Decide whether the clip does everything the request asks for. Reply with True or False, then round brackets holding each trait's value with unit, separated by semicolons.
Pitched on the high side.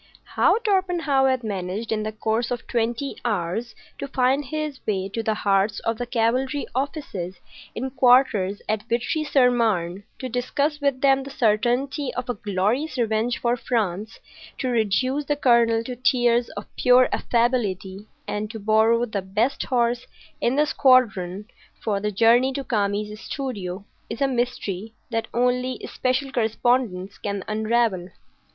True (235 Hz)